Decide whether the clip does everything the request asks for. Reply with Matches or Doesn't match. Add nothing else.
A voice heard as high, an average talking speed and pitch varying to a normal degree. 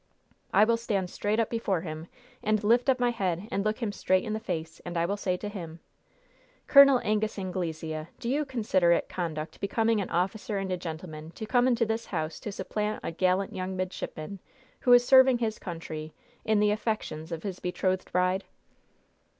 Matches